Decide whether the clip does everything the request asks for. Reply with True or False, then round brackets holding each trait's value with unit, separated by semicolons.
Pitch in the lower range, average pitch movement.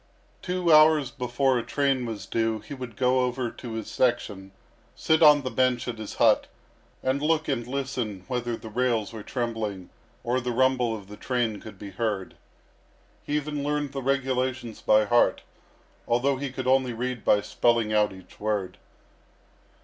True (125 Hz; 3.1 semitones)